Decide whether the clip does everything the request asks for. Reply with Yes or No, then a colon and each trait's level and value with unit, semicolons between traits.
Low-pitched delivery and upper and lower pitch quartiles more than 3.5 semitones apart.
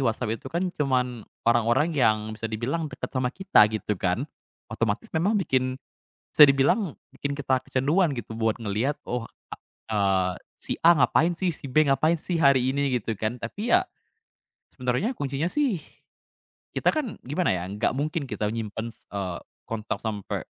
Yes: low, 130 Hz; wide, 5.6 semitones